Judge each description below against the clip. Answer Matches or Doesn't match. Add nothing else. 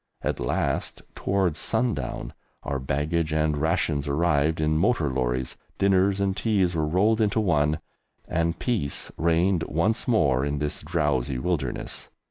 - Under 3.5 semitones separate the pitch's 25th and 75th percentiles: Doesn't match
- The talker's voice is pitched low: Matches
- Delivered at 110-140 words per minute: Matches